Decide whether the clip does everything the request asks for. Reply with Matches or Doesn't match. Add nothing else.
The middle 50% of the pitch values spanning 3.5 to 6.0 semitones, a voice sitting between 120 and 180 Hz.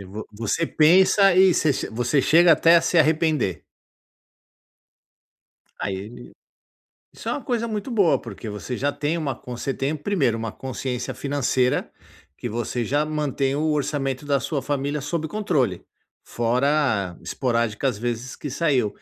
Matches